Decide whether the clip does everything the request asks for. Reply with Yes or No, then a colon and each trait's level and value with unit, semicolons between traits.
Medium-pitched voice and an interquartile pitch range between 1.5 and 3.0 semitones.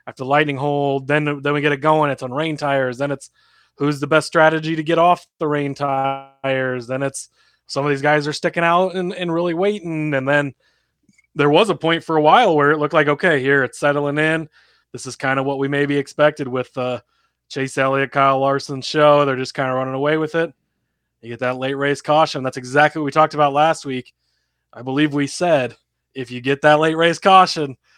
Yes: medium, 145 Hz; narrow, 2.4 semitones